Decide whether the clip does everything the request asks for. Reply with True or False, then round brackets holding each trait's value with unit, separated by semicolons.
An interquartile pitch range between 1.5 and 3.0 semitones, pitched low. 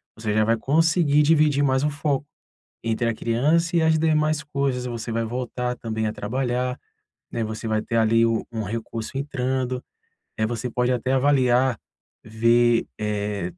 False (3.7 semitones; 125 Hz)